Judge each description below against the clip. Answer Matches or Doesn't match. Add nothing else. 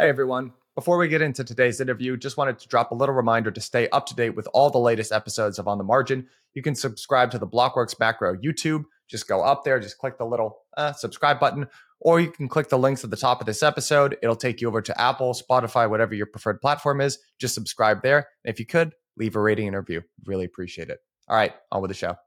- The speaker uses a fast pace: Matches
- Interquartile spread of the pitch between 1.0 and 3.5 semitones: Doesn't match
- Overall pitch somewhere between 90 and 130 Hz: Matches